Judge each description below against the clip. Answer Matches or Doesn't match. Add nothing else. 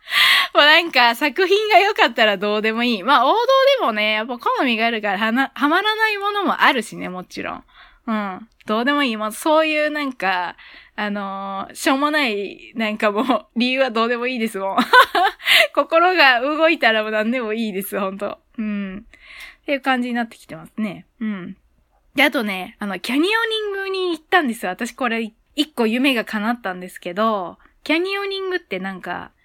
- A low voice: Doesn't match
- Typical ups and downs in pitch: Doesn't match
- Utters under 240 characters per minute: Doesn't match